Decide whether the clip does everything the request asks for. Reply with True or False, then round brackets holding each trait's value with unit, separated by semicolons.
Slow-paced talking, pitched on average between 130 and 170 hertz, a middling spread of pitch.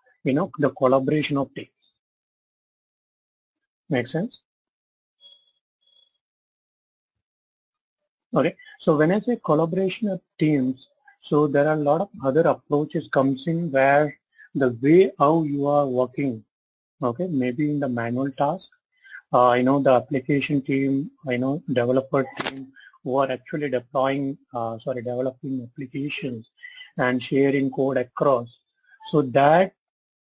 True (125 wpm; 140 Hz; 3.9 semitones)